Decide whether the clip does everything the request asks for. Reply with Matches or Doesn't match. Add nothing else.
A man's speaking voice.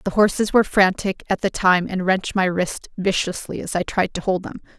Doesn't match